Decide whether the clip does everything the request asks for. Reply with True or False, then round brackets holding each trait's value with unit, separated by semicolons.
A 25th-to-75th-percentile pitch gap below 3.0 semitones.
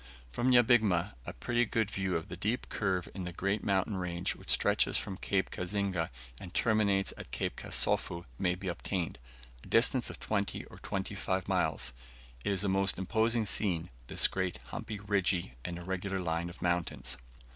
True (2.6 semitones)